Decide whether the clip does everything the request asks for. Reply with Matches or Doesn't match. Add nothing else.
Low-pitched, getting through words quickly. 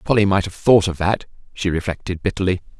Doesn't match